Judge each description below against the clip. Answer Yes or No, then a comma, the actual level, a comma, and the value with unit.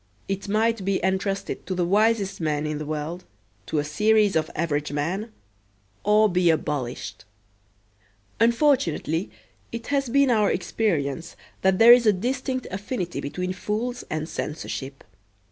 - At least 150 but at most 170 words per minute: No, average, 140 wpm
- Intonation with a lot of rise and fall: Yes, wide, 6.0 semitones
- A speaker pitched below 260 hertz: Yes, high, 190 Hz